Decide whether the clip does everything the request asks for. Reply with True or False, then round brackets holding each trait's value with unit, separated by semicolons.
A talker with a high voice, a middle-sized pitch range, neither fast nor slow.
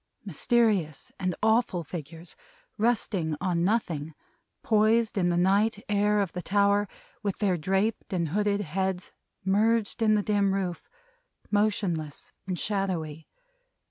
False (195 Hz; 3.3 semitones; 125 wpm)